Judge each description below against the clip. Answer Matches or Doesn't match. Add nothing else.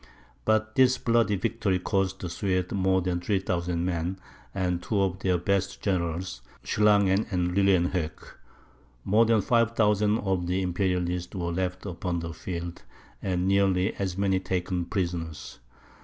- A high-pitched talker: Doesn't match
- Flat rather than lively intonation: Matches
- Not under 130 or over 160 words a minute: Matches